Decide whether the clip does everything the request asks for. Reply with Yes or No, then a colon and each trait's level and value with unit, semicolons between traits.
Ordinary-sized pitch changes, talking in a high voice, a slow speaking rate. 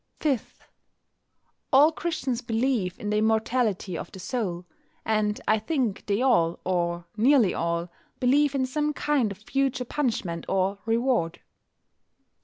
No: wide, 5.7 semitones; high, 225 Hz; slow, 130 wpm